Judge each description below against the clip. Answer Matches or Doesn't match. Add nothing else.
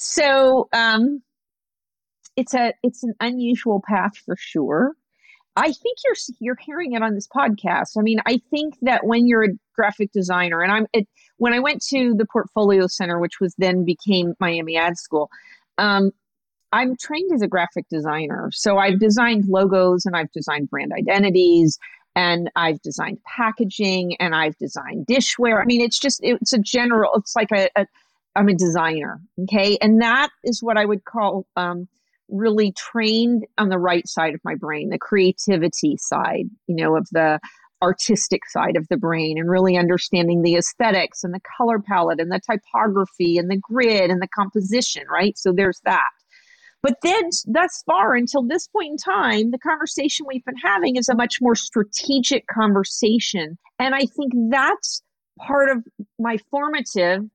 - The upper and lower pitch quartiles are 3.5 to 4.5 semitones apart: Doesn't match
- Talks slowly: Doesn't match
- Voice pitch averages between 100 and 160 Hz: Doesn't match